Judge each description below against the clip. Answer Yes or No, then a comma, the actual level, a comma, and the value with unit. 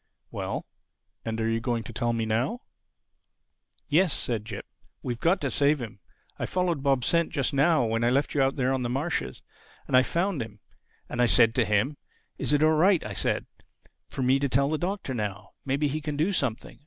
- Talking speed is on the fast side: Yes, fast, 210 wpm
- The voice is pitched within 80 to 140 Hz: Yes, low, 135 Hz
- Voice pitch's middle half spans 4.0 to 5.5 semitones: Yes, average, 4.7 semitones